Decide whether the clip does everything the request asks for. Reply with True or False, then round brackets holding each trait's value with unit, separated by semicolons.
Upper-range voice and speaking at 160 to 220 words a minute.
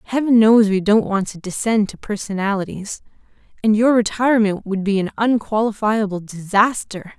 False (210 Hz; 140 wpm)